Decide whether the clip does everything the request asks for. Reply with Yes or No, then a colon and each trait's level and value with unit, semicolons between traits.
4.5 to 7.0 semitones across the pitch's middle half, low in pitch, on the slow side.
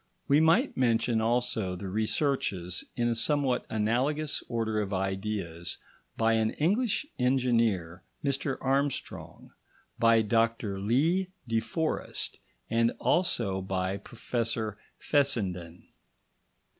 Yes: average, 5.1 semitones; low, 115 Hz; slow, 105 wpm